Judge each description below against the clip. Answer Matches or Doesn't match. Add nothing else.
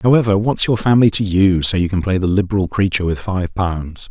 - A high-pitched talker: Doesn't match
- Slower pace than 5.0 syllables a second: Doesn't match